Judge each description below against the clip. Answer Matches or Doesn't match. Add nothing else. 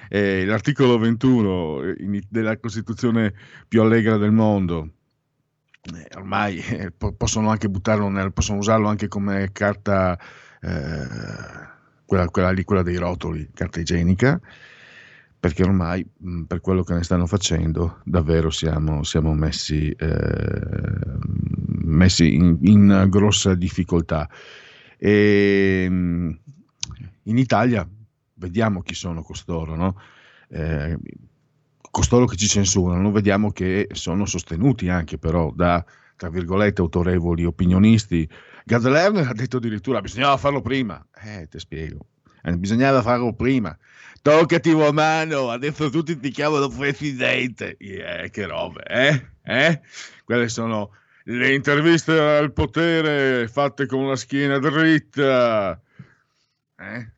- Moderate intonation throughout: Doesn't match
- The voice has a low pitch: Matches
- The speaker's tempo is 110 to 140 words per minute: Matches